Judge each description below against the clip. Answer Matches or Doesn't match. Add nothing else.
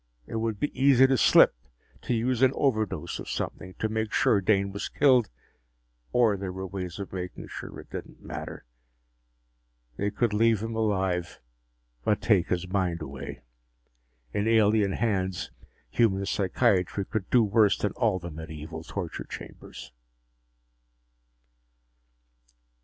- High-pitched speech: Doesn't match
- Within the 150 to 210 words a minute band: Doesn't match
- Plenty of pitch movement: Doesn't match